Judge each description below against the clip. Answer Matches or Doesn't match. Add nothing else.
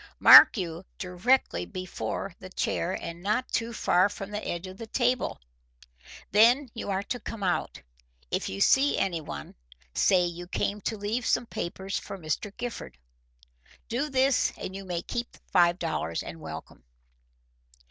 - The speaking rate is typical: Matches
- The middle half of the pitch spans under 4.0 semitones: Doesn't match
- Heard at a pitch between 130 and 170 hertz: Doesn't match